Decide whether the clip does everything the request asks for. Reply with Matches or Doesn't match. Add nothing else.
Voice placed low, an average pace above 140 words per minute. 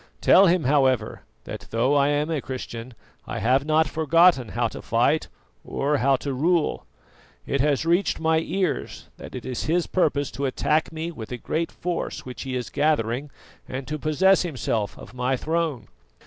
Doesn't match